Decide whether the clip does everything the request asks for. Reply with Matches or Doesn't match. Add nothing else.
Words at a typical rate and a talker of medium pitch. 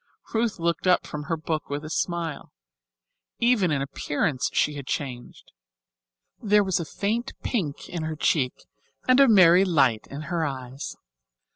Matches